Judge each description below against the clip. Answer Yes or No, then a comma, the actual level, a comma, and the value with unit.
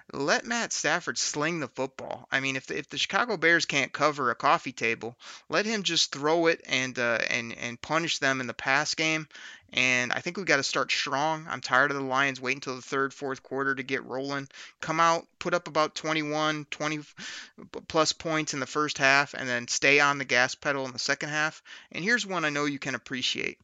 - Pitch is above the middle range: No, medium, 140 Hz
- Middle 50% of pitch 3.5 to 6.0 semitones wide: No, average, 3.1 semitones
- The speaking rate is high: Yes, fast, 225 wpm